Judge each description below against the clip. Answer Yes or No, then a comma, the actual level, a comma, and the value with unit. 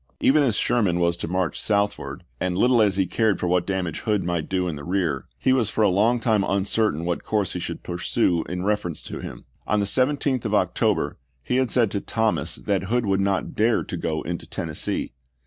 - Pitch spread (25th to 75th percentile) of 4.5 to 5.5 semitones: No, average, 4.1 semitones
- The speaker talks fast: Yes, fast, 215 wpm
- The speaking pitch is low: Yes, low, 100 Hz